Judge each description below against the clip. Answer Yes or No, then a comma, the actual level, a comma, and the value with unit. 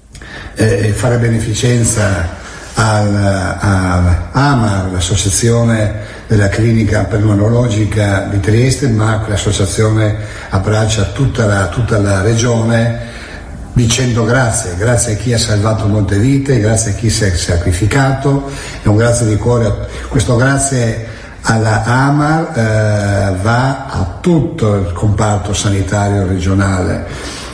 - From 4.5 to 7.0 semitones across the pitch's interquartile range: No, average, 2.8 semitones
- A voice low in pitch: Yes, low, 110 Hz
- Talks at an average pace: No, slow, 110 wpm